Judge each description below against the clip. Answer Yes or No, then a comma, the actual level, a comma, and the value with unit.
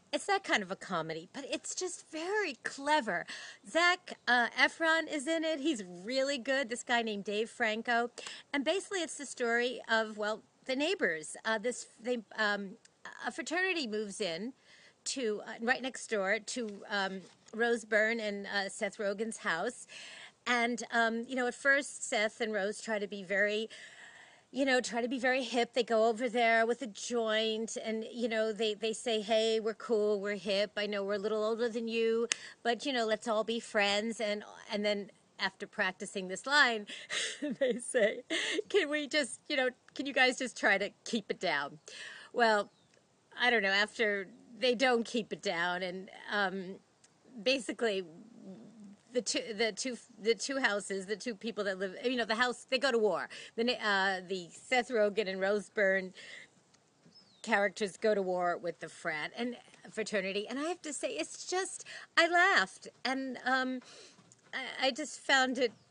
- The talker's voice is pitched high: Yes, high, 230 Hz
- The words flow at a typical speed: Yes, average, 180 wpm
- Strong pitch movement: No, average, 3.9 semitones